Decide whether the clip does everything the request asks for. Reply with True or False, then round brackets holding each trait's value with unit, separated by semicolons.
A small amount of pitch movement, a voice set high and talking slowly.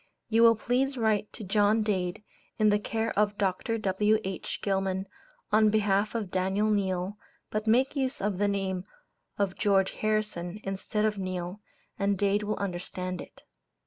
False (2.1 semitones; 205 Hz; 155 wpm)